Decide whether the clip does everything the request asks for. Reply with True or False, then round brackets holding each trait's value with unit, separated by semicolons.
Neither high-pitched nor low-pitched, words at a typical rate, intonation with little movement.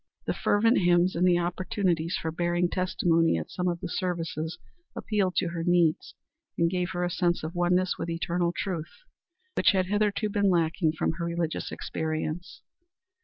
True (175 Hz; 170 wpm; 1.7 semitones)